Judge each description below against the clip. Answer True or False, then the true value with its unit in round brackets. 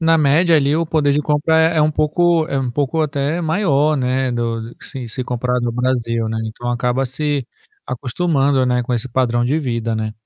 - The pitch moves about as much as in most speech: True (3.9 semitones)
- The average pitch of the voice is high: False (135 Hz)